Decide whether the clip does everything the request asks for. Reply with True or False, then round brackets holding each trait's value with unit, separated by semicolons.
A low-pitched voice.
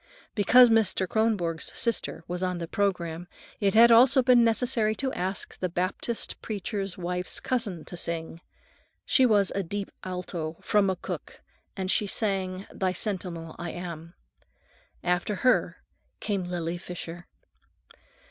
False (190 Hz)